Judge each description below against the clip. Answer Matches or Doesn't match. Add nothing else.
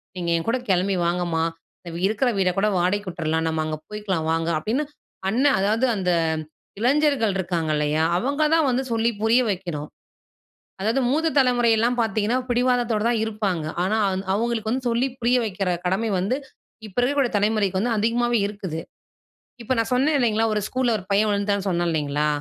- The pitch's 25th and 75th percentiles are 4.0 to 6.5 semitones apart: Matches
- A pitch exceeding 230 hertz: Doesn't match